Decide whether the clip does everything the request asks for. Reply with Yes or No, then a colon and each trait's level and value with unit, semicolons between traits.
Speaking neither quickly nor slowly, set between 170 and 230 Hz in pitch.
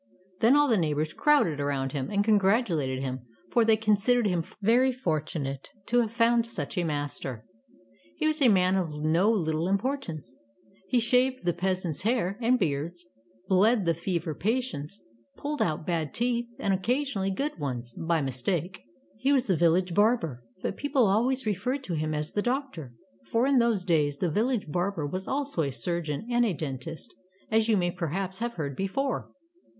Yes: average, 175 wpm; high, 190 Hz